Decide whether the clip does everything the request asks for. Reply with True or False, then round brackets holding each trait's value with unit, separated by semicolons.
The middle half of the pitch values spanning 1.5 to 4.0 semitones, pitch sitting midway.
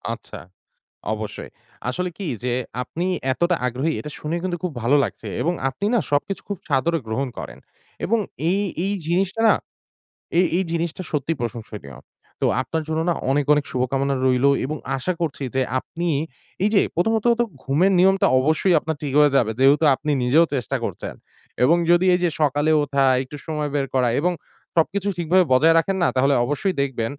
False (4.8 semitones; 155 Hz)